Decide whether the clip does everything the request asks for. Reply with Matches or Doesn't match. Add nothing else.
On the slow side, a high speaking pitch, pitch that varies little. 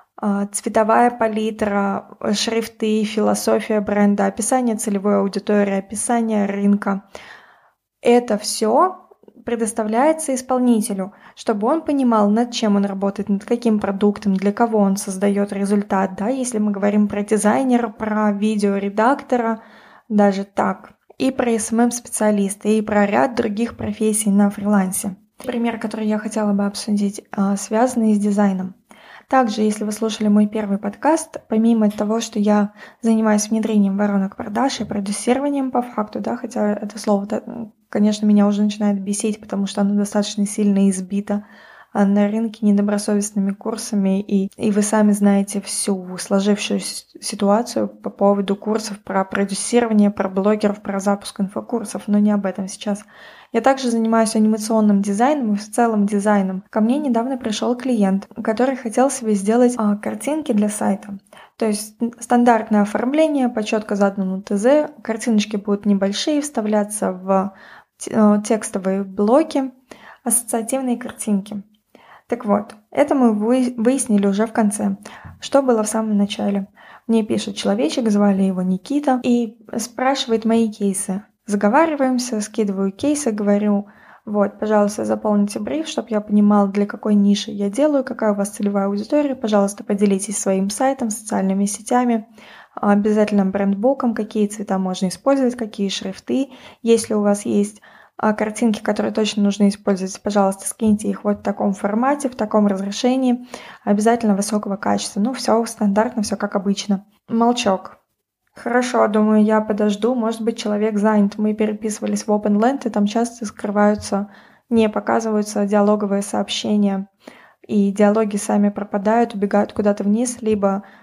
Doesn't match